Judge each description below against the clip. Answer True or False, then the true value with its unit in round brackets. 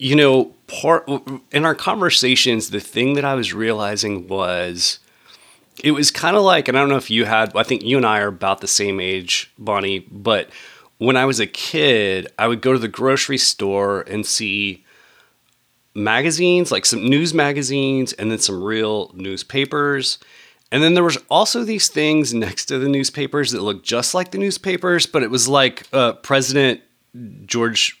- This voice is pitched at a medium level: False (130 Hz)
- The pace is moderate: True (180 wpm)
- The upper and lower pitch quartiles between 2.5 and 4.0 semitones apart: False (5.2 semitones)